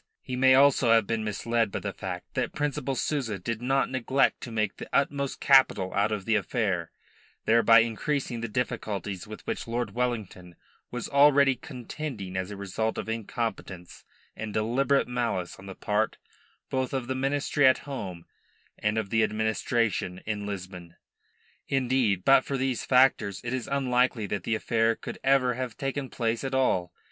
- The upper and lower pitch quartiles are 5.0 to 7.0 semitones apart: No, average, 4.1 semitones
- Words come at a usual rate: Yes, average, 170 wpm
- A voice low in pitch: Yes, low, 115 Hz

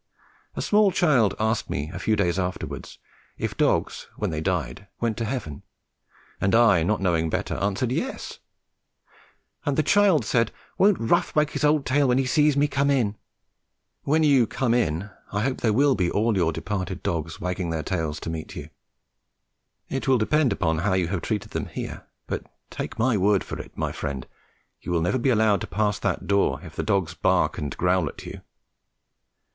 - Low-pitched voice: Yes, low, 105 Hz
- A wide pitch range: Yes, wide, 6.7 semitones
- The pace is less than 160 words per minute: No, average, 190 wpm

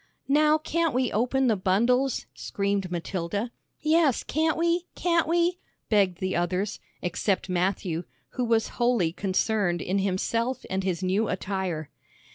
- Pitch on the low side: No, high, 205 Hz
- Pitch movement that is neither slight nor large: No, wide, 6.0 semitones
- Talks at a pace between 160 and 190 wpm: No, slow, 135 wpm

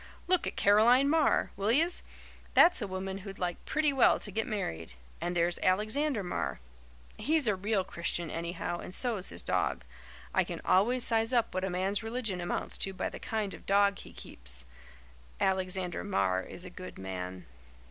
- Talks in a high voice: Yes, high, 195 Hz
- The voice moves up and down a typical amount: Yes, average, 4.2 semitones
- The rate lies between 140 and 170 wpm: No, average, 180 wpm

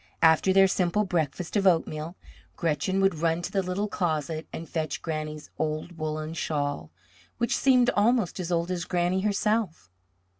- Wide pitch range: No, average, 3.6 semitones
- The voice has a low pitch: No, medium, 175 Hz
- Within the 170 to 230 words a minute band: No, average, 155 wpm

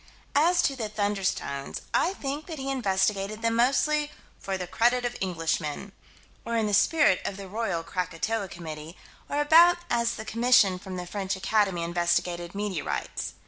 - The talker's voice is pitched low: No, high, 205 Hz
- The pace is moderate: Yes, average, 160 wpm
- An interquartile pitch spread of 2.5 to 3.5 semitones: No, average, 5.0 semitones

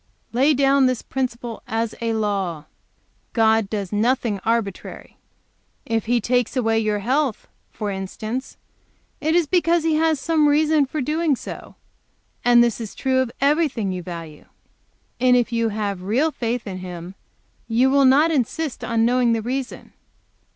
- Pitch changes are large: No, average, 4.3 semitones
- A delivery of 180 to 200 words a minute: No, average, 155 wpm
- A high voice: Yes, high, 240 Hz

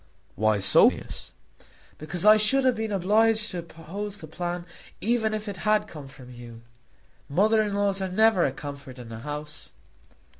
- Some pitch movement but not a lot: No, wide, 6.4 semitones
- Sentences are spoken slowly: No, average, 175 wpm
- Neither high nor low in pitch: Yes, medium, 180 Hz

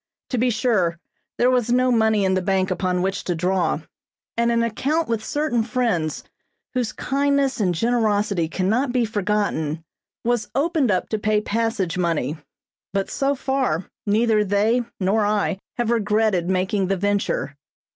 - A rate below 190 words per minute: Yes, average, 155 wpm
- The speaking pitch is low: No, high, 215 Hz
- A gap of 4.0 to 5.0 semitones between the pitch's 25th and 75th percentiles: Yes, average, 4.3 semitones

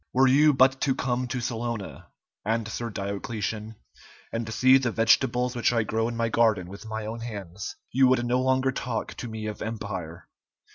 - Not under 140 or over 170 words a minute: No, average, 180 wpm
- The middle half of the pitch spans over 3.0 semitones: No, narrow, 2.6 semitones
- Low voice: Yes, low, 115 Hz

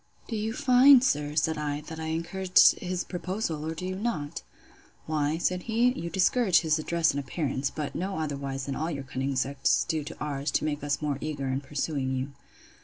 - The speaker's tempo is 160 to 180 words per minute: No, average, 200 wpm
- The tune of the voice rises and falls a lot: No, average, 4.3 semitones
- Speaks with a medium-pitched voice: Yes, medium, 155 Hz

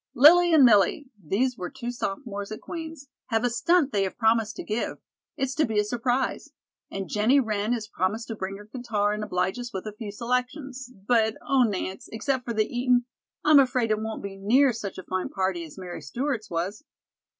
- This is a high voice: Yes, high, 225 Hz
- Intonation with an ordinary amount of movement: Yes, average, 3.9 semitones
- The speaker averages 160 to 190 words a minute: No, fast, 205 wpm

